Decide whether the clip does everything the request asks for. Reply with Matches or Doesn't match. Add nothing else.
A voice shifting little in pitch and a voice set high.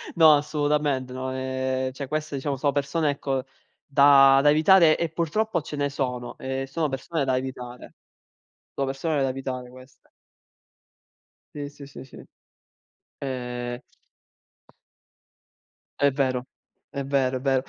Doesn't match